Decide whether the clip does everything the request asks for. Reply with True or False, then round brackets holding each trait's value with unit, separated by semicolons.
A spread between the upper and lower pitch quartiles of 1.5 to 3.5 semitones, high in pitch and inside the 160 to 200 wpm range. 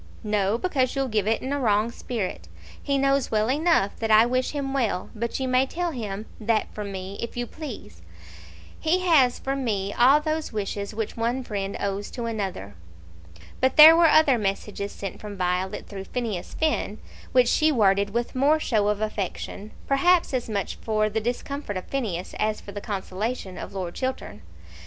False (4.9 semitones; 225 Hz; 185 wpm)